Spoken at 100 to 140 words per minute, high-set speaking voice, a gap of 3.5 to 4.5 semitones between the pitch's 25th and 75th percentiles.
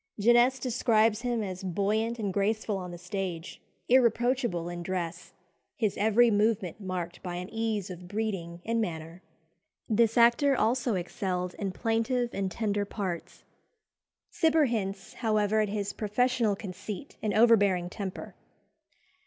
Yes: slow, 135 wpm; high, 210 Hz; average, 3.8 semitones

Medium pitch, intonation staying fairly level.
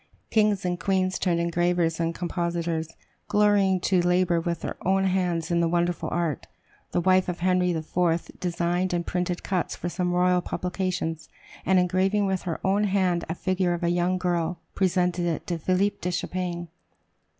Yes: medium, 180 Hz; narrow, 1.4 semitones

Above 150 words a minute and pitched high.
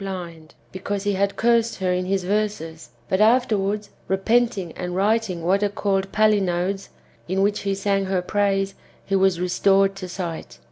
Yes: average, 160 wpm; high, 195 Hz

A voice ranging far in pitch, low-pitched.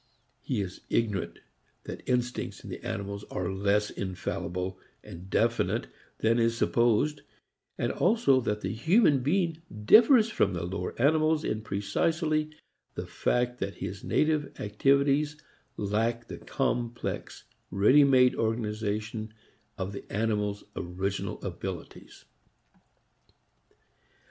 Yes: wide, 5.8 semitones; low, 115 Hz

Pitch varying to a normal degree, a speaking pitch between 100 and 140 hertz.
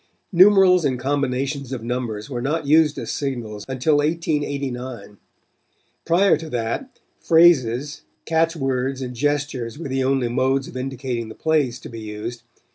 Yes: average, 3.7 semitones; low, 135 Hz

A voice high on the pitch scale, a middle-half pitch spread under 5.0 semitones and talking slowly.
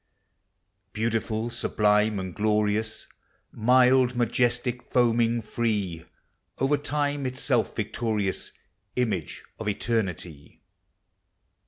No: low, 115 Hz; average, 2.8 semitones; slow, 75 wpm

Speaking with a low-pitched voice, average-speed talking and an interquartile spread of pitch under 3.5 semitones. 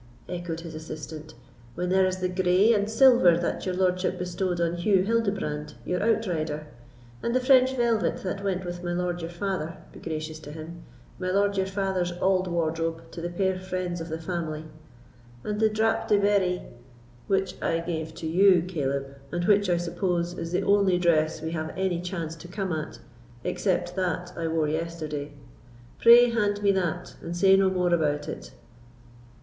No: medium, 180 Hz; average, 175 wpm; average, 2.7 semitones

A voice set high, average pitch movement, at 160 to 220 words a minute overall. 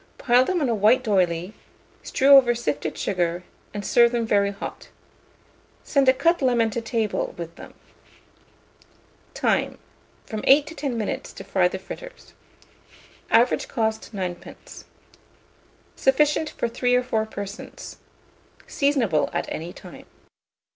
No: high, 230 Hz; average, 4.7 semitones; slow, 135 wpm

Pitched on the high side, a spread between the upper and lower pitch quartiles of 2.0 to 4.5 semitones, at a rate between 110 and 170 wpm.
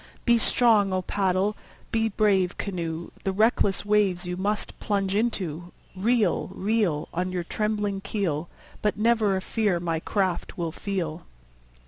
Yes: high, 195 Hz; average, 3.0 semitones; average, 140 wpm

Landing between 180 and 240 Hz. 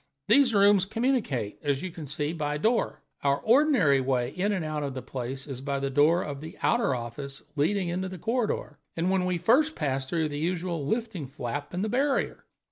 No: medium, 160 Hz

